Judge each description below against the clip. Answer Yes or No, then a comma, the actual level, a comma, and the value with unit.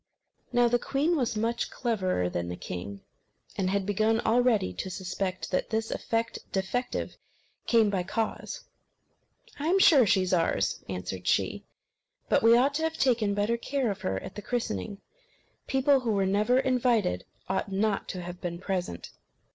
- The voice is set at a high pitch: Yes, high, 210 Hz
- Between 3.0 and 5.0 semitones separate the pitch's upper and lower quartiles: Yes, average, 4.7 semitones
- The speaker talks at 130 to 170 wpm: Yes, average, 165 wpm